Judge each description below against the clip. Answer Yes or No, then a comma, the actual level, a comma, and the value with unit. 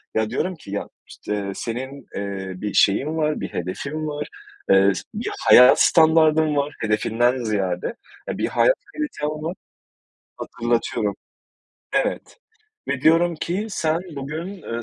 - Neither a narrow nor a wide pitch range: No, wide, 6.7 semitones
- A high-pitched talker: No, medium, 140 Hz